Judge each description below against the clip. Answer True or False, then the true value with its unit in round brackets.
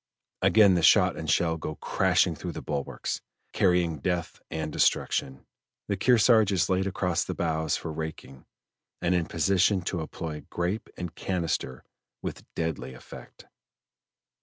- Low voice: True (85 Hz)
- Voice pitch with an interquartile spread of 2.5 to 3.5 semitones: True (2.9 semitones)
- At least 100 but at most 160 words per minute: True (140 wpm)